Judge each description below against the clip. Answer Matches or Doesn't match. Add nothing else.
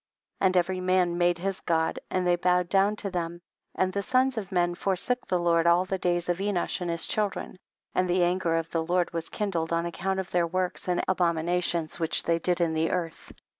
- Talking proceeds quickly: Matches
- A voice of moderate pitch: Matches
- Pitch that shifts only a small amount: Matches